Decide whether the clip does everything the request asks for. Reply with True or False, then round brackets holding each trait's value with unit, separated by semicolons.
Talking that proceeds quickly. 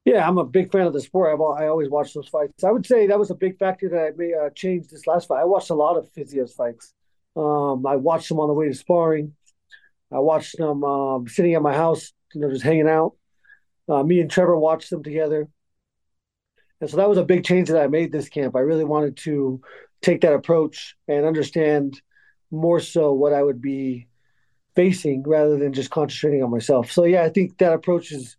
True (225 wpm)